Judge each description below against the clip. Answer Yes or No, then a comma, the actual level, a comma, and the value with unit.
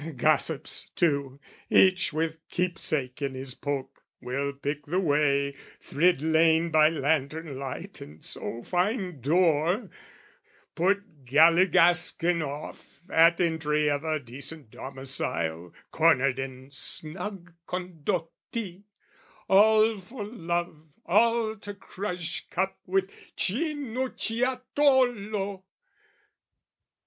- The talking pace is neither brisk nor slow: No, slow, 95 wpm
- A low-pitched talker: No, medium, 165 Hz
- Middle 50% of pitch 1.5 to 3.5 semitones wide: No, average, 5.3 semitones